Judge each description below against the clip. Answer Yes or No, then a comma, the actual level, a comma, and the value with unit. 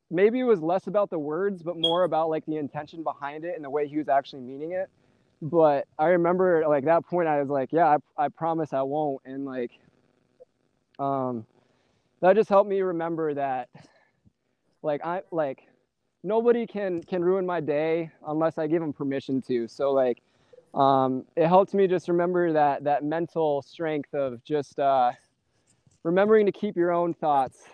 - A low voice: No, medium, 160 Hz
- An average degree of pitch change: Yes, average, 4.0 semitones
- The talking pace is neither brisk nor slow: Yes, average, 180 wpm